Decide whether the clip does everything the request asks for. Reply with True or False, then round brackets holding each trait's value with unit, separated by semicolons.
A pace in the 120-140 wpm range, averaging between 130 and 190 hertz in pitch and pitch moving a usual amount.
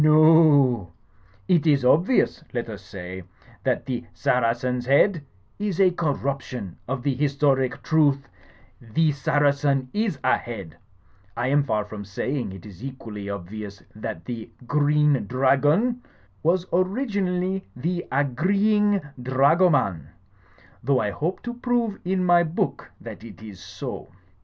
False (135 wpm; 140 Hz; 6.6 semitones)